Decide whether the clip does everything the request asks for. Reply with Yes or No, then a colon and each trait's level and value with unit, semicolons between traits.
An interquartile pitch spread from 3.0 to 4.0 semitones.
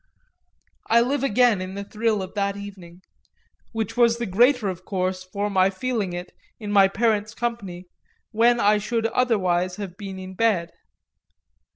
Yes: average, 3.6 semitones